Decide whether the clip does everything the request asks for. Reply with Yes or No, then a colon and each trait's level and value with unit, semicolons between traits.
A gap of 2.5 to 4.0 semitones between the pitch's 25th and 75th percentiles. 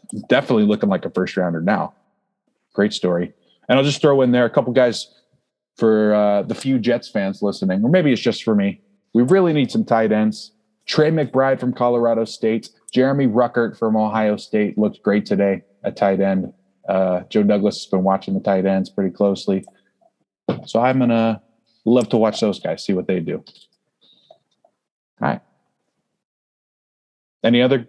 Yes: average, 3.6 semitones